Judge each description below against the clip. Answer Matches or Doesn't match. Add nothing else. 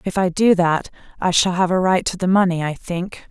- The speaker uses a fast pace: Matches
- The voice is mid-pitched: Matches